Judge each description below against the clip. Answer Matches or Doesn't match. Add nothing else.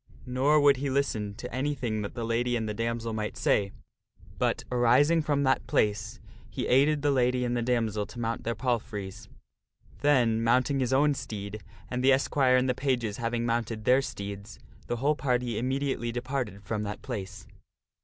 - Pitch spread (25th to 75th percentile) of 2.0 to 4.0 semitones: Matches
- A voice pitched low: Matches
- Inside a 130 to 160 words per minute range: Doesn't match